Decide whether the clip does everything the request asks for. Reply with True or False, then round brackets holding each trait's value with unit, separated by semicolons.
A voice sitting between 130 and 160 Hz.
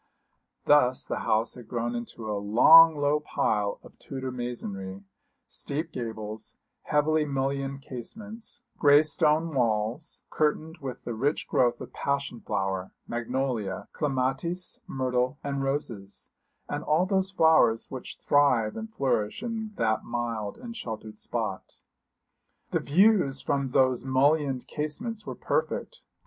True (135 Hz)